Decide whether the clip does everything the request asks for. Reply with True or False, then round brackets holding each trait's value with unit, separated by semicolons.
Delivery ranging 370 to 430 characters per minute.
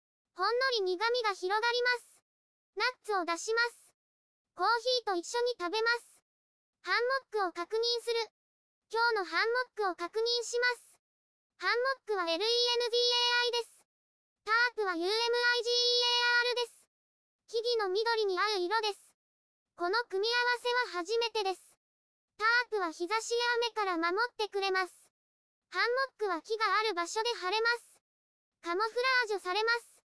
False (300 characters per minute)